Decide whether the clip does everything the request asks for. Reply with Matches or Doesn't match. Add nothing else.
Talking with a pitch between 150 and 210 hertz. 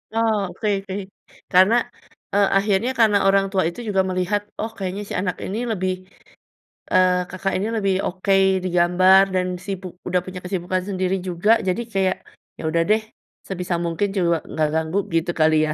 Matches